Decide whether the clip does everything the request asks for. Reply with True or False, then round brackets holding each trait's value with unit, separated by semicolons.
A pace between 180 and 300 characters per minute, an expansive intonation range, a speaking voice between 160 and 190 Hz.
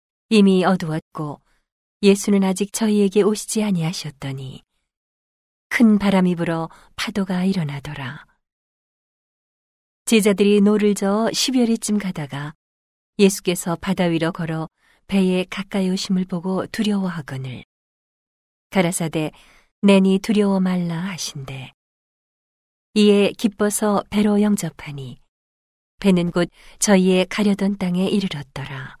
False (250 characters per minute; 4.4 semitones; 185 Hz)